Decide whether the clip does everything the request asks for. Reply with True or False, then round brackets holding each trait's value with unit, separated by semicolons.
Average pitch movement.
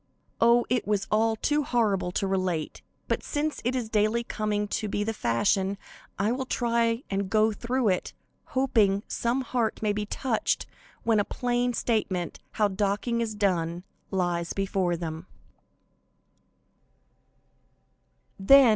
True (3.4 semitones)